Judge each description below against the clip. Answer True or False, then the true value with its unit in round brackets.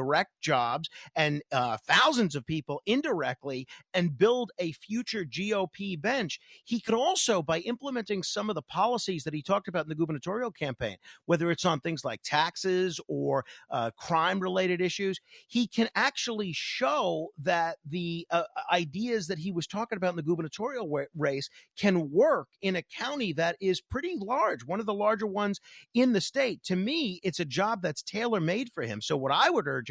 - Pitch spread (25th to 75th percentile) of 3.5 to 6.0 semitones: True (5.0 semitones)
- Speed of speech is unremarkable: True (185 wpm)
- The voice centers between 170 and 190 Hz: True (185 Hz)